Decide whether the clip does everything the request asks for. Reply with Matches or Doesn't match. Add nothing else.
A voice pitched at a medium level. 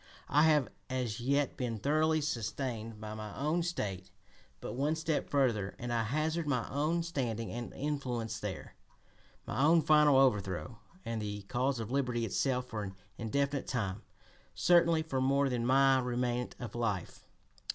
Doesn't match